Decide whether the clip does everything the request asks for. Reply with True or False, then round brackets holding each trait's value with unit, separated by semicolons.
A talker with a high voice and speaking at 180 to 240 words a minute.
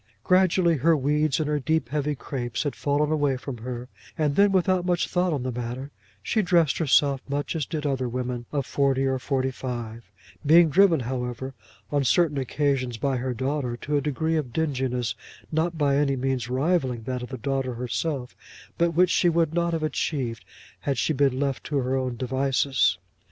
False (140 Hz; 190 wpm)